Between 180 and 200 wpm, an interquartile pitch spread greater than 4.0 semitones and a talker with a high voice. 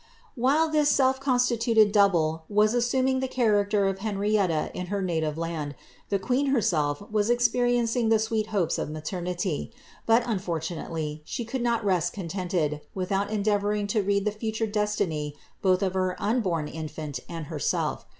No: average, 155 wpm; average, 5.1 semitones; high, 205 Hz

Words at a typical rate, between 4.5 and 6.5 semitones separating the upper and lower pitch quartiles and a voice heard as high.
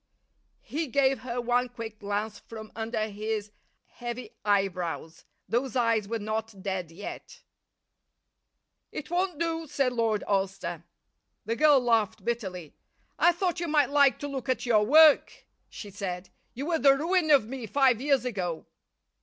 Yes: average, 150 wpm; average, 5.2 semitones; high, 235 Hz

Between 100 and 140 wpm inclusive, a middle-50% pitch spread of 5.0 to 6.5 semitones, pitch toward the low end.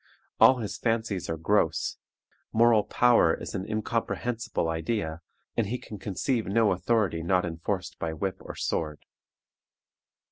Yes: slow, 135 wpm; wide, 5.5 semitones; low, 100 Hz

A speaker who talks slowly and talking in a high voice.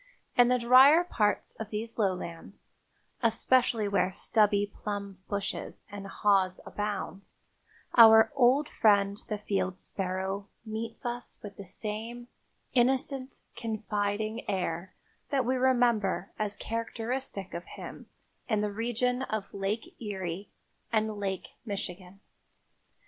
Yes: slow, 115 wpm; high, 210 Hz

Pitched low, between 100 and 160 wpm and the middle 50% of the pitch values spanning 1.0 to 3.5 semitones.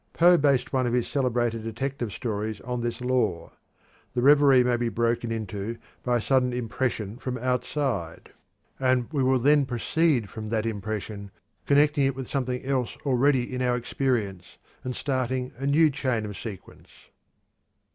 Yes: low, 125 Hz; average, 155 wpm; average, 2.8 semitones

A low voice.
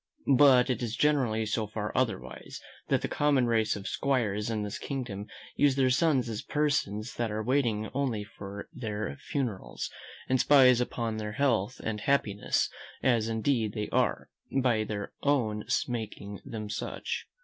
Yes: low, 115 Hz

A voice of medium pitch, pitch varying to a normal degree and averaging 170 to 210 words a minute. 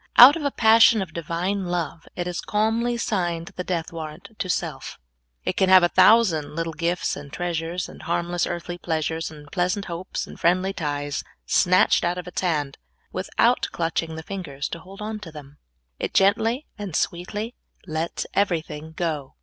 Yes: medium, 175 Hz; average, 3.2 semitones; average, 175 wpm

